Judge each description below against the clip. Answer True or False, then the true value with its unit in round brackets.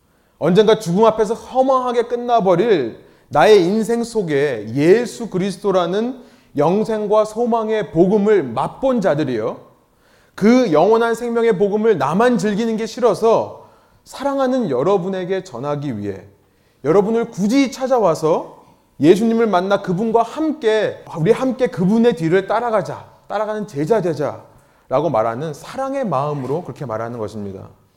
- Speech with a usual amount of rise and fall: False (6.3 semitones)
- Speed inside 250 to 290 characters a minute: False (305 characters per minute)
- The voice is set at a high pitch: True (215 Hz)